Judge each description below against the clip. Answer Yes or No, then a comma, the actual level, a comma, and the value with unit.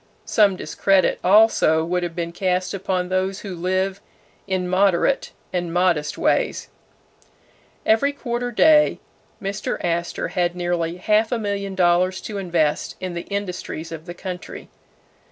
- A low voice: No, medium, 185 Hz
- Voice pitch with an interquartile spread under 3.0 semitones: Yes, narrow, 2.4 semitones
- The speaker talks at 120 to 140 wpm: Yes, slow, 135 wpm